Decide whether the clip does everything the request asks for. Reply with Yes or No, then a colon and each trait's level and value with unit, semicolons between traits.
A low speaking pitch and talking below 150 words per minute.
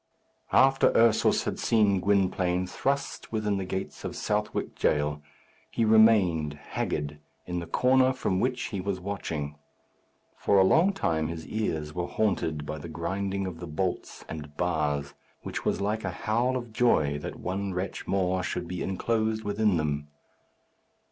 No: very low, 95 Hz; average, 155 wpm